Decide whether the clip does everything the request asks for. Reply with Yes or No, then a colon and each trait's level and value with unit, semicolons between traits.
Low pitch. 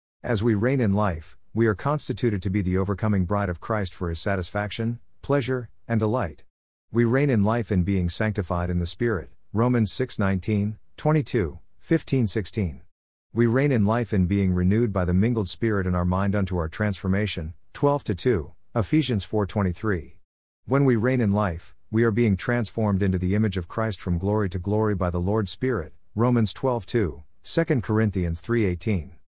Yes: low, 105 Hz